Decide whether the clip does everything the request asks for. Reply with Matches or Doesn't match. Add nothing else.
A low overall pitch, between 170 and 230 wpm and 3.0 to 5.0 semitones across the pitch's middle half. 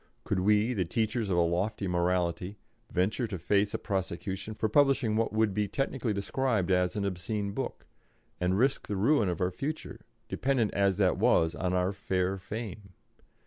Matches